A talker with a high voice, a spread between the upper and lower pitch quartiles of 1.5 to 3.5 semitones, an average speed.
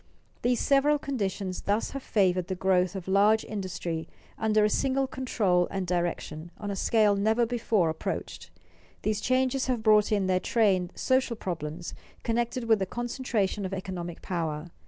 No: high, 205 Hz; average, 4.2 semitones; average, 155 wpm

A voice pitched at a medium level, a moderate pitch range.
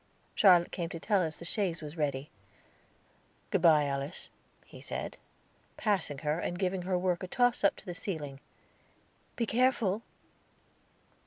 Yes: medium, 175 Hz; average, 4.3 semitones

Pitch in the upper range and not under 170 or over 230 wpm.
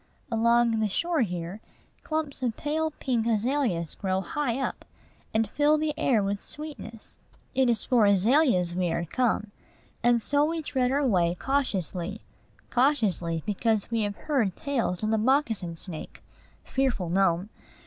No: high, 225 Hz; average, 150 wpm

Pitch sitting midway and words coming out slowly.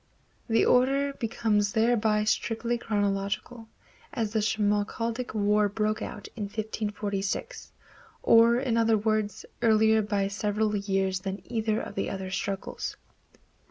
No: high, 215 Hz; slow, 125 wpm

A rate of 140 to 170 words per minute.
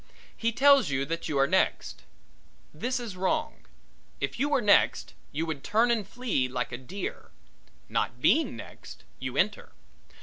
Yes: average, 160 wpm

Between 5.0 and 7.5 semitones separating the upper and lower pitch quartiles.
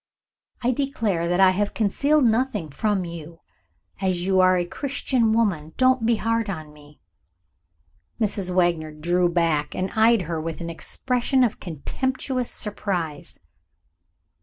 Yes: wide, 5.5 semitones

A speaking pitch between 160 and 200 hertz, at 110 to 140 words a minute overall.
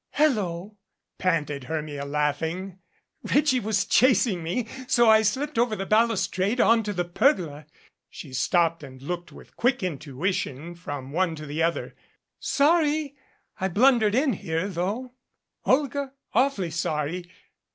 Yes: medium, 185 Hz; slow, 135 wpm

